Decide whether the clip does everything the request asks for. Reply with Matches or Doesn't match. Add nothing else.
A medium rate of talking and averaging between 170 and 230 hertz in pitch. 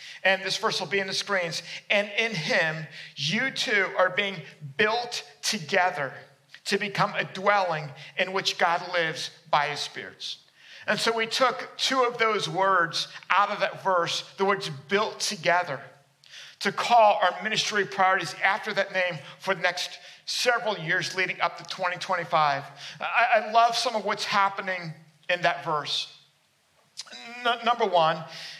Matches